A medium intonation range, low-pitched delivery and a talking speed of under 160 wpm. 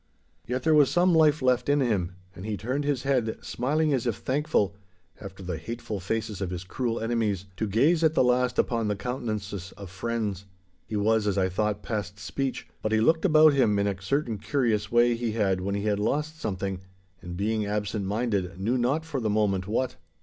No: average, 4.3 semitones; low, 110 Hz; fast, 205 wpm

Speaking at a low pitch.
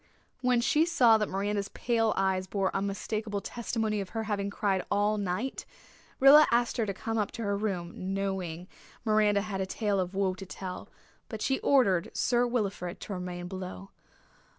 No: high, 200 Hz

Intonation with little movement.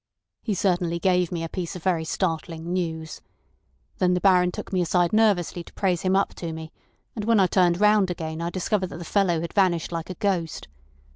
Yes: narrow, 2.2 semitones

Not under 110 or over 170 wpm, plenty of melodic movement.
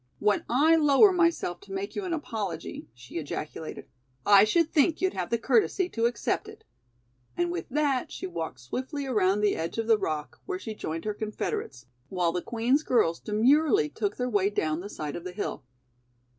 No: average, 190 wpm; wide, 8.4 semitones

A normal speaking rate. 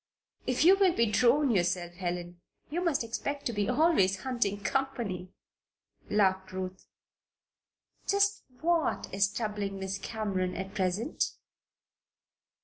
No: slow, 125 wpm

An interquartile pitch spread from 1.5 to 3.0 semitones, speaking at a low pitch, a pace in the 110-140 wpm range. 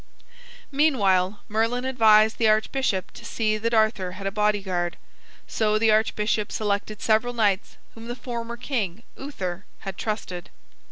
No: narrow, 2.6 semitones; high, 215 Hz; slow, 135 wpm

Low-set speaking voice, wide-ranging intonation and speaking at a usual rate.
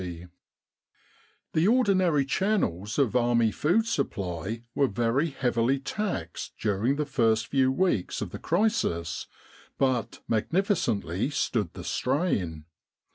No: low, 125 Hz; wide, 7.7 semitones; slow, 120 wpm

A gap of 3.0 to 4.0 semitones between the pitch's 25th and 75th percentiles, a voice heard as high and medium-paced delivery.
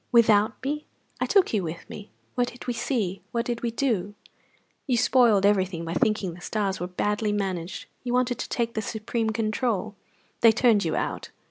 Yes: average, 3.5 semitones; high, 215 Hz; average, 190 wpm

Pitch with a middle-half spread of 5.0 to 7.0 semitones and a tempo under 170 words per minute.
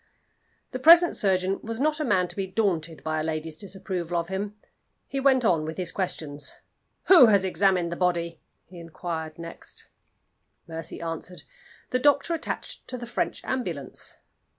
Yes: wide, 5.5 semitones; average, 160 wpm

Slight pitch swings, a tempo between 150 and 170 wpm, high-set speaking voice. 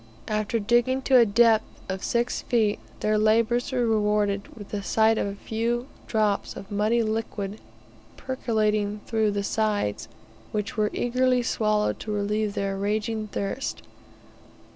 No: narrow, 2.0 semitones; average, 140 wpm; high, 215 Hz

